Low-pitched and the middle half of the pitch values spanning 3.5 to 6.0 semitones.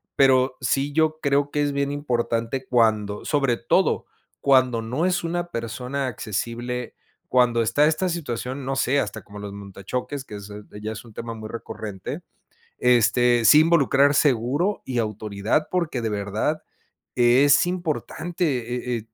Yes: low, 125 Hz; average, 4.1 semitones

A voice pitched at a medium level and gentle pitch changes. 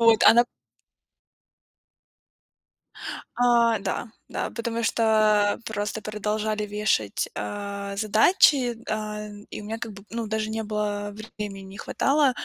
No: high, 215 Hz; narrow, 1.9 semitones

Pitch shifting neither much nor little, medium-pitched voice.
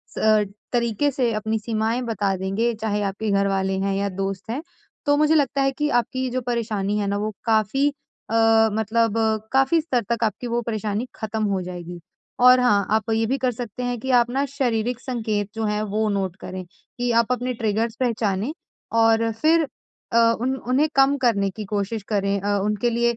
No: average, 3.3 semitones; high, 225 Hz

